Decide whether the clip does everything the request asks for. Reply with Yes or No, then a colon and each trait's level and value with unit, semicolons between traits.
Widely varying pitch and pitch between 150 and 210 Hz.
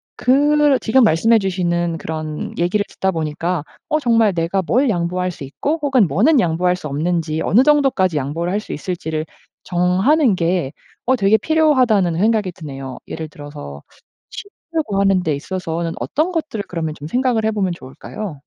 Yes: wide, 6.2 semitones; medium, 185 Hz